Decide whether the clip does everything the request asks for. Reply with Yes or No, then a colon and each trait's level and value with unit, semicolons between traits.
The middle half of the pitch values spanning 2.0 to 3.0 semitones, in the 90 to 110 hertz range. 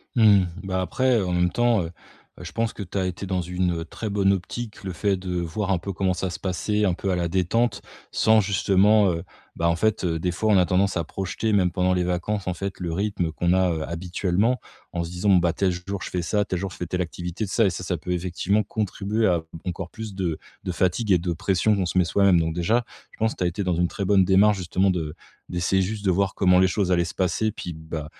Yes: narrow, 2.4 semitones; very low, 95 Hz